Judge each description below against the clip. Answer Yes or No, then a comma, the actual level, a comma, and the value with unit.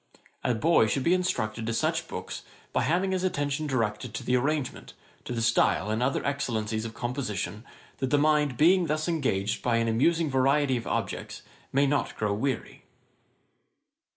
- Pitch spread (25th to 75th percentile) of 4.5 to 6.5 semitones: Yes, average, 4.8 semitones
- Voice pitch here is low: Yes, low, 130 Hz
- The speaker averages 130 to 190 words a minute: Yes, average, 170 wpm